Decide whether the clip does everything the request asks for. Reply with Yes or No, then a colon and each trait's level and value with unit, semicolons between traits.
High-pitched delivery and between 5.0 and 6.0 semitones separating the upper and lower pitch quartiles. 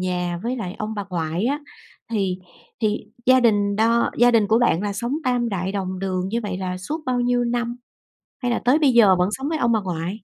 No: high, 215 Hz; average, 4.5 semitones